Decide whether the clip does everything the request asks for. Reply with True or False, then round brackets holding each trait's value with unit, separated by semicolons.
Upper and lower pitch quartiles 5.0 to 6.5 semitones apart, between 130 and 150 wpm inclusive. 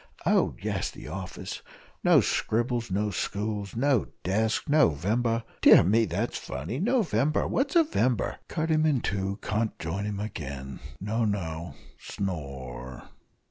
True (5.5 semitones; 140 wpm)